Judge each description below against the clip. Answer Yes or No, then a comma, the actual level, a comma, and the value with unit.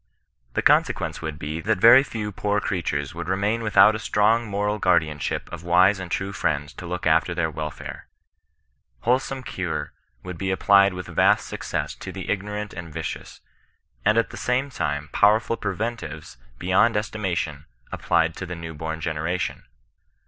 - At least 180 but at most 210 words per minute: No, average, 165 wpm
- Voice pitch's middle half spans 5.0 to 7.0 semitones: No, average, 4.5 semitones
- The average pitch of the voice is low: Yes, very low, 95 Hz